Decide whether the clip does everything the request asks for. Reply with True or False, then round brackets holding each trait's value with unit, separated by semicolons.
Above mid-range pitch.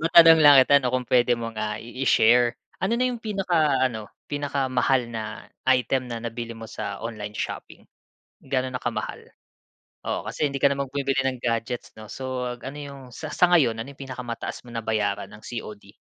False (125 Hz)